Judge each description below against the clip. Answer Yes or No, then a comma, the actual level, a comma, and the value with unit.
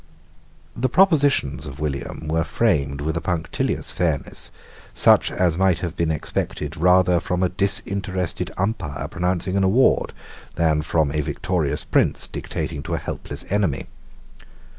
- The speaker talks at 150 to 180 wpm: No, average, 140 wpm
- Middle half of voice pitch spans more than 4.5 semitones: No, average, 3.6 semitones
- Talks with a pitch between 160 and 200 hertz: No, very low, 85 Hz